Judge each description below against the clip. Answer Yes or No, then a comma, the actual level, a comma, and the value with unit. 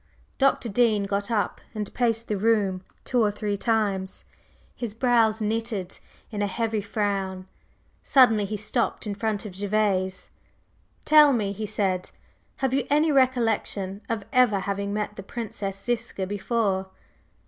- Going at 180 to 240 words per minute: No, average, 145 wpm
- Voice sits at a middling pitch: No, high, 210 Hz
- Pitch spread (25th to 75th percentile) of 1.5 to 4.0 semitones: Yes, average, 2.7 semitones